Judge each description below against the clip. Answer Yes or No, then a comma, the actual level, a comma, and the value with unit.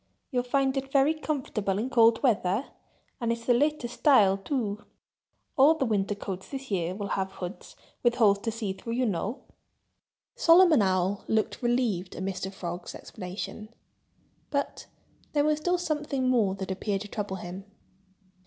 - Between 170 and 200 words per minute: No, average, 155 wpm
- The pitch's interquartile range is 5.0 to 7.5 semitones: Yes, wide, 5.6 semitones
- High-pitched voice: Yes, high, 225 Hz